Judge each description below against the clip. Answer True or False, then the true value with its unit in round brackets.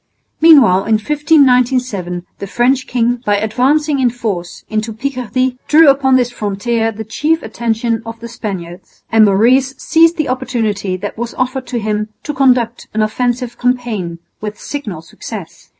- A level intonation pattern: False (3.4 semitones)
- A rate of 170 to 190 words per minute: False (150 wpm)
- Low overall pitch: False (235 Hz)